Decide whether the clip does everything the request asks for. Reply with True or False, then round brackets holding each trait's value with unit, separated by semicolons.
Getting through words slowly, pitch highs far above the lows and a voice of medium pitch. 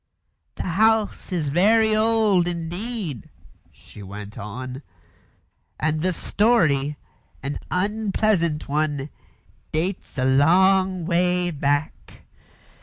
True (95 wpm; 5.7 semitones; 175 Hz)